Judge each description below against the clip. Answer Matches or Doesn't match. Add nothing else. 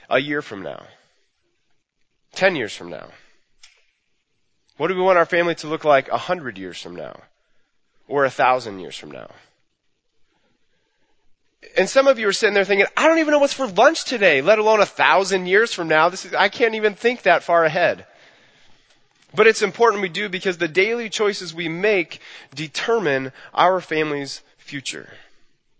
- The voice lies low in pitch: Doesn't match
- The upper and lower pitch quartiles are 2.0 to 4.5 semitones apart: Doesn't match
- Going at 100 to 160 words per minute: Doesn't match